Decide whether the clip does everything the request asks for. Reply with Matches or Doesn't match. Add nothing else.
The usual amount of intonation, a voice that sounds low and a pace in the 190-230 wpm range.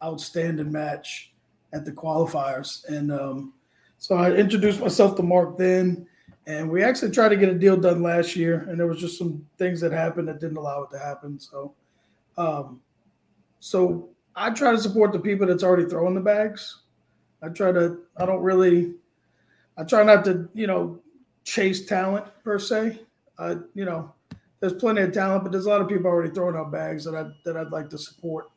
Doesn't match